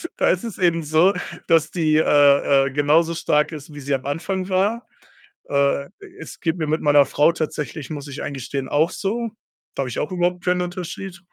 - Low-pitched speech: No, medium, 155 Hz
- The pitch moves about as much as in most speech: Yes, average, 3.8 semitones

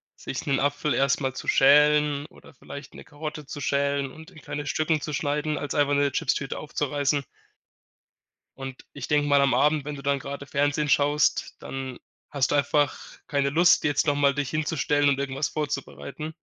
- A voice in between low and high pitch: Yes, medium, 145 Hz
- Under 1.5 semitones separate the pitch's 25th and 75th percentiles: Yes, narrow, 1.1 semitones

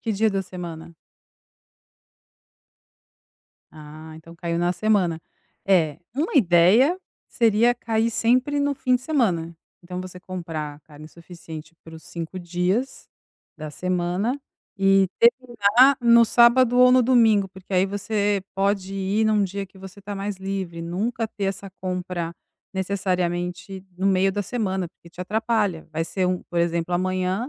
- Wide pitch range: No, average, 4.1 semitones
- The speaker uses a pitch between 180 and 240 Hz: Yes, high, 190 Hz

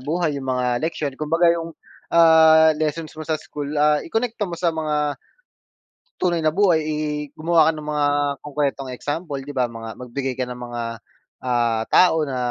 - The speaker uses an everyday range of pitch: Yes, average, 3.1 semitones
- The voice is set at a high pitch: No, medium, 150 Hz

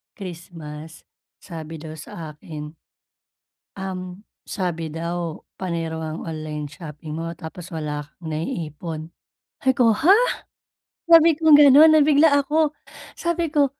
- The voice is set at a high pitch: No, medium, 170 Hz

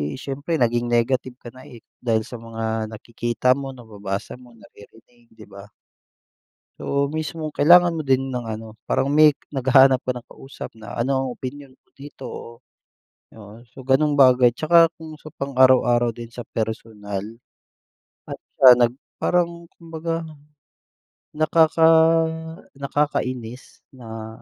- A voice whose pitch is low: Yes, low, 125 Hz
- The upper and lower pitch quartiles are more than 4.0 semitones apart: No, average, 3.7 semitones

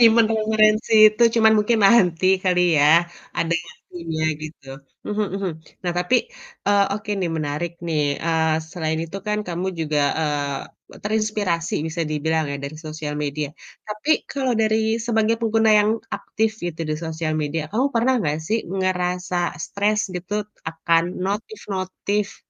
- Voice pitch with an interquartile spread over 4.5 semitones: Yes, average, 5.1 semitones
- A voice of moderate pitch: Yes, medium, 180 Hz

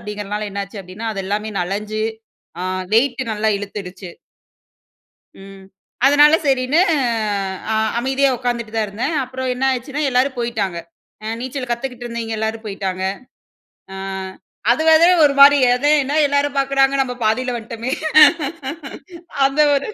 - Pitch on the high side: Yes, high, 240 Hz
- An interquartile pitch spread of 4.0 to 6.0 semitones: Yes, average, 4.4 semitones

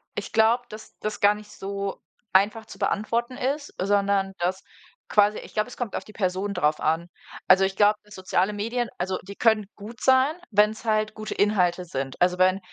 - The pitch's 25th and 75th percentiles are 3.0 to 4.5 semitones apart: No, narrow, 2.5 semitones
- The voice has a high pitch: Yes, high, 205 Hz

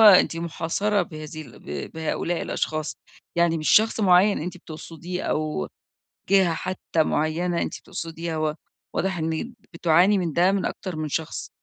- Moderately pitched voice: Yes, medium, 170 Hz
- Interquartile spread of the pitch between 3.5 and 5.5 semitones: No, average, 2.7 semitones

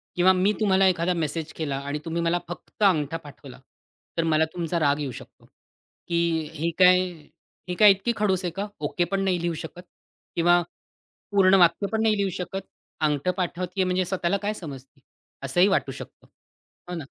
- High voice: No, medium, 175 Hz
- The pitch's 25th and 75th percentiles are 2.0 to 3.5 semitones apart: Yes, average, 2.8 semitones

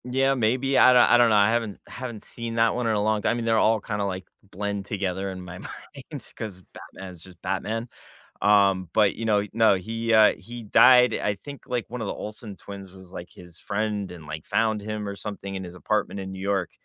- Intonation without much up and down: No, average, 3.0 semitones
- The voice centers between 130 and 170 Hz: No, low, 105 Hz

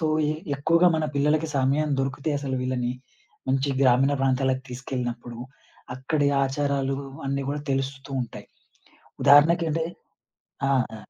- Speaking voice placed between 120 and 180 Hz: Yes, low, 135 Hz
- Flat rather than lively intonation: Yes, narrow, 1.9 semitones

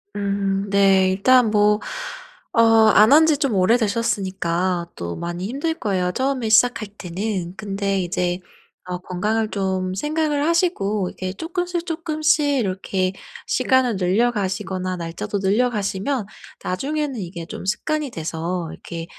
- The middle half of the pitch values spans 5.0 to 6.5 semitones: Yes, wide, 5.5 semitones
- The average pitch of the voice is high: Yes, high, 200 Hz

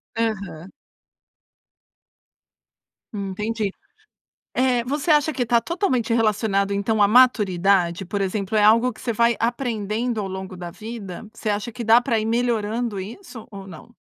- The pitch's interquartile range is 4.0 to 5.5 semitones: No, average, 3.2 semitones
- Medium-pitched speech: No, high, 220 Hz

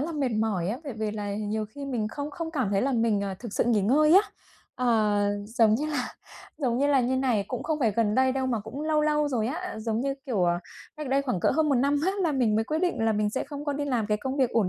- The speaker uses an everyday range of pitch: Yes, average, 4.8 semitones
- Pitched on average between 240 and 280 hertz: Yes, very high, 250 Hz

